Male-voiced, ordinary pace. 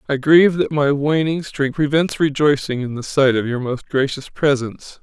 Yes: male; average, 190 wpm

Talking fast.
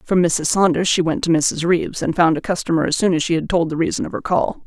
Yes: fast, 295 wpm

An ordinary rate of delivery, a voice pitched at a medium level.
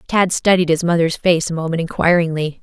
Yes: average, 185 wpm; medium, 170 Hz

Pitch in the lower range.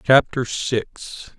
Yes: low, 125 Hz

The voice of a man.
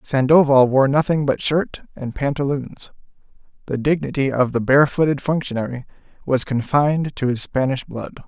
Yes: male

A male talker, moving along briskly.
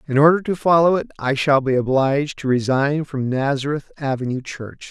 No: male; average, 185 wpm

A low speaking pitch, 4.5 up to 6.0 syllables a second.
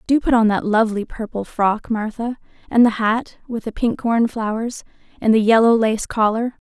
No: high, 225 Hz; 4.9 syllables/s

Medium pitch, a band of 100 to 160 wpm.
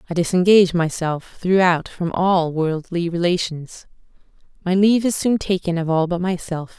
Yes: medium, 175 Hz; average, 150 wpm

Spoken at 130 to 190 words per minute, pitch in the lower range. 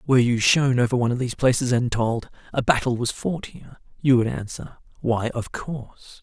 No: fast, 205 wpm; low, 125 Hz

